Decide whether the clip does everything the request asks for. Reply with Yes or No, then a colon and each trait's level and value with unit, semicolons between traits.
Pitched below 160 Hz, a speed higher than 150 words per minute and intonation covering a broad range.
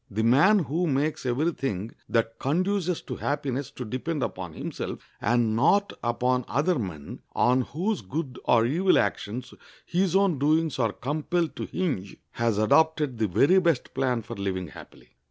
Yes: low, 135 Hz; average, 160 wpm; wide, 6.1 semitones